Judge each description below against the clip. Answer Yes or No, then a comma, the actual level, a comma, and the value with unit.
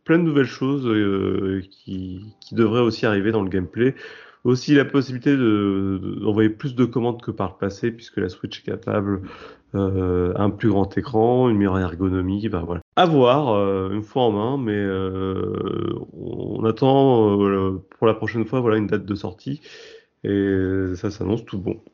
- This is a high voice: No, low, 105 Hz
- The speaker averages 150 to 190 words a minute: Yes, average, 180 wpm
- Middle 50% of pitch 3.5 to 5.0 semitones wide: Yes, average, 4.0 semitones